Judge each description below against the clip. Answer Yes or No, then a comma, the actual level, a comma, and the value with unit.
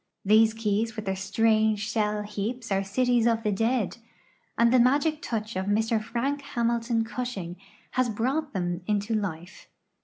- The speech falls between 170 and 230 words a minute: No, average, 155 wpm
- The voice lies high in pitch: Yes, high, 225 Hz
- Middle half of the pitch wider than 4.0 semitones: No, average, 2.7 semitones